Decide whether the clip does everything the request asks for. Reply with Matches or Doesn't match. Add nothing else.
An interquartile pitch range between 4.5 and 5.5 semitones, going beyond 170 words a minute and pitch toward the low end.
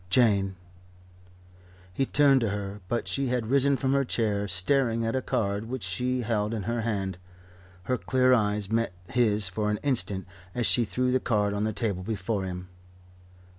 Doesn't match